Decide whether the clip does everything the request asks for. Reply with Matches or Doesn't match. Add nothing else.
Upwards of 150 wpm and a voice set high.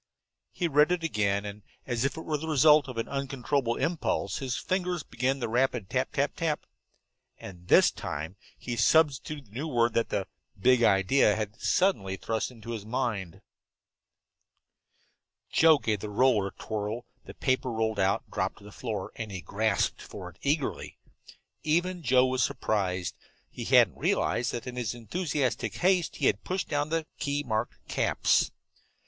Doesn't match